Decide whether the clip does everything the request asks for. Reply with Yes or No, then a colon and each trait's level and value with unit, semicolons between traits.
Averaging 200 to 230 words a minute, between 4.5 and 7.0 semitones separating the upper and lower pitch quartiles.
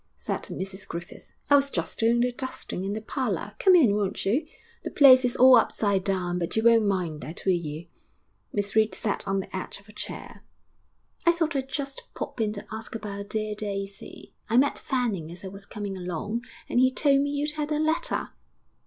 Yes: fast, 205 wpm; average, 4.9 semitones